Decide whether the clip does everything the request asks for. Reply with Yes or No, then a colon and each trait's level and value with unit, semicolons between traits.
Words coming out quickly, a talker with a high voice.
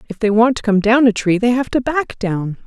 Yes: fast, 295 wpm; high, 225 Hz